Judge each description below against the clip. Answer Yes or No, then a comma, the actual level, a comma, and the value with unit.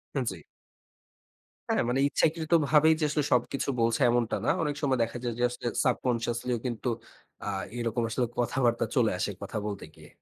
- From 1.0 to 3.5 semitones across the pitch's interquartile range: Yes, average, 3.2 semitones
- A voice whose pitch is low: Yes, low, 120 Hz